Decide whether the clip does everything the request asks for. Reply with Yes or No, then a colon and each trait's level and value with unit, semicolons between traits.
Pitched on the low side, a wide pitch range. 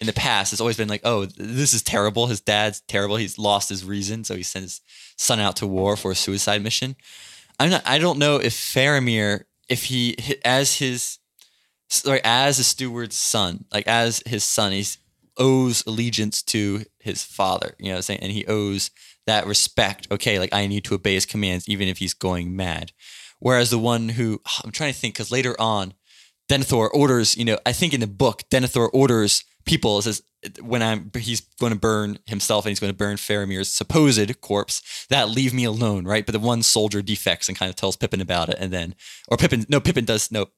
No: low, 110 Hz; average, 3.3 semitones